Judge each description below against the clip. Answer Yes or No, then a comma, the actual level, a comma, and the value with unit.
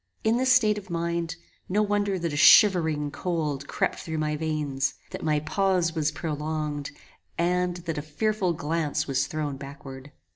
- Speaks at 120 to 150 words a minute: No, average, 160 wpm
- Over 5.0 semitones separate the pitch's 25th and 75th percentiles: No, average, 3.5 semitones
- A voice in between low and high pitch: Yes, medium, 160 Hz